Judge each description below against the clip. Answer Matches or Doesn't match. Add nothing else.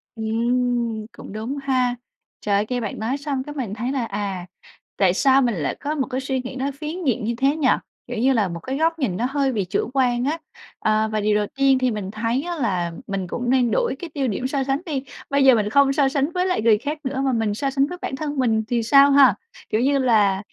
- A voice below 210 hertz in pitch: Doesn't match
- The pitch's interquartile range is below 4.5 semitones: Matches